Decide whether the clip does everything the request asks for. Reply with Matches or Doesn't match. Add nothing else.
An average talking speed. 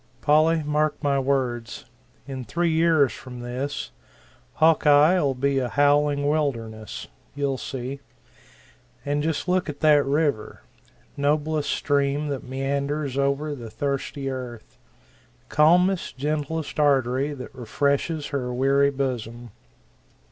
Doesn't match